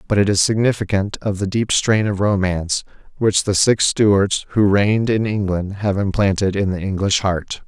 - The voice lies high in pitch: No, low, 100 Hz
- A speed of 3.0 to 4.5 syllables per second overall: No, 4.9 syllables/s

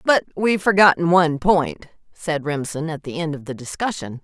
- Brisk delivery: No, average, 185 wpm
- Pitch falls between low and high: Yes, medium, 160 Hz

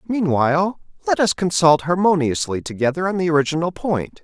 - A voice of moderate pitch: Yes, medium, 170 Hz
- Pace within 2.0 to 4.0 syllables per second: No, 5.5 syllables/s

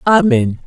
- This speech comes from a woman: Yes, female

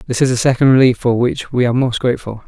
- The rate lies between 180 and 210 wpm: No, fast, 265 wpm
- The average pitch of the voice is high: No, low, 125 Hz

